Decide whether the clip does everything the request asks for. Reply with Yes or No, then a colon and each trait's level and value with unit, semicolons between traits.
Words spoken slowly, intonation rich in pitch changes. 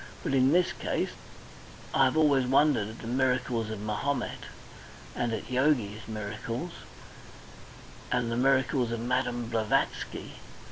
No: slow, 125 wpm; average, 3.1 semitones